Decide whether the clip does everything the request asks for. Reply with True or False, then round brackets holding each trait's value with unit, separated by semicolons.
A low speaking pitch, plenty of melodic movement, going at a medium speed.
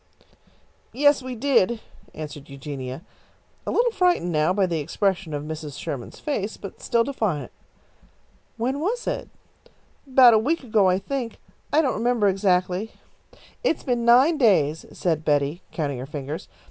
False (195 Hz; 8.7 semitones; 145 wpm)